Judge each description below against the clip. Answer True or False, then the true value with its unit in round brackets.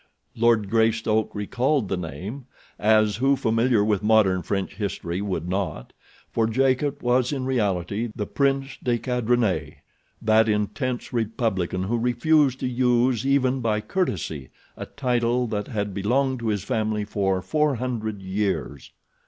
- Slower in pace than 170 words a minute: True (135 wpm)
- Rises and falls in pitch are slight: False (3.6 semitones)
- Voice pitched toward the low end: True (110 Hz)